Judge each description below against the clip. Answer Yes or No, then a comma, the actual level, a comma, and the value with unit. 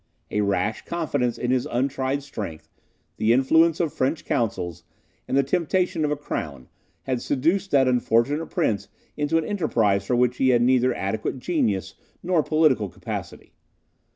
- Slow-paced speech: No, average, 155 wpm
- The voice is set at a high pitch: No, low, 130 Hz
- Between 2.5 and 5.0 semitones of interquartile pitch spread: No, wide, 5.4 semitones